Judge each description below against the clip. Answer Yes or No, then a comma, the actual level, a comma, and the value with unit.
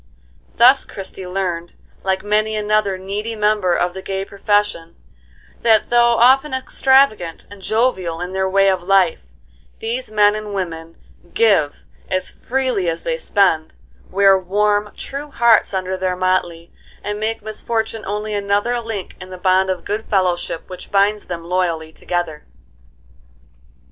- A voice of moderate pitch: No, high, 195 Hz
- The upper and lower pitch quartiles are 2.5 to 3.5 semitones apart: Yes, average, 2.9 semitones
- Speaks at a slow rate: No, average, 145 wpm